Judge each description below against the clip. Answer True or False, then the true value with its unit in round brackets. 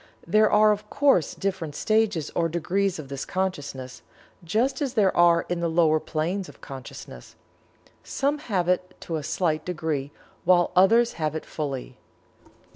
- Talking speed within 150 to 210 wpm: True (155 wpm)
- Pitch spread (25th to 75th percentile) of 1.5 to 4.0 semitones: False (4.5 semitones)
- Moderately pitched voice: True (175 Hz)